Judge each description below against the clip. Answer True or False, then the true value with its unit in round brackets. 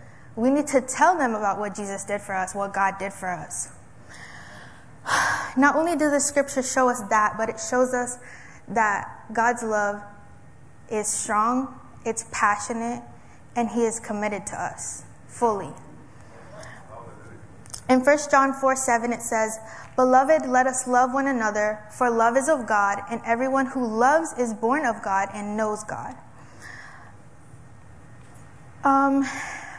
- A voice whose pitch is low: False (230 Hz)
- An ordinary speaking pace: True (145 wpm)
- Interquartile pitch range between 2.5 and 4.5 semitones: True (4.1 semitones)